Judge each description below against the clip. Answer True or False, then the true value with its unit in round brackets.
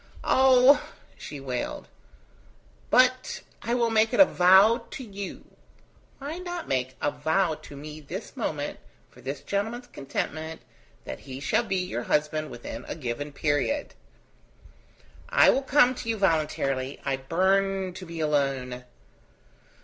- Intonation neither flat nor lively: False (8.7 semitones)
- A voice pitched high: False (170 Hz)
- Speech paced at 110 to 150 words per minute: True (140 wpm)